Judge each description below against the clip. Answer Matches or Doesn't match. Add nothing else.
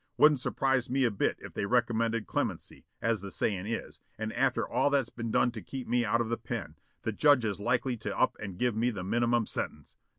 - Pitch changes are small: Matches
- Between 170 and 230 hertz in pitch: Doesn't match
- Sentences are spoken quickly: Matches